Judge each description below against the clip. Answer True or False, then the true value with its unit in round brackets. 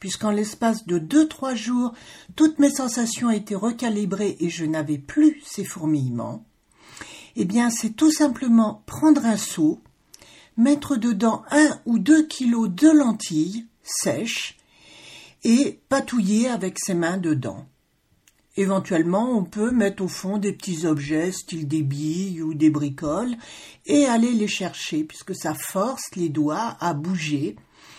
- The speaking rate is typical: False (140 wpm)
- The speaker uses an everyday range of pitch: False (6.7 semitones)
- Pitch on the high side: True (205 Hz)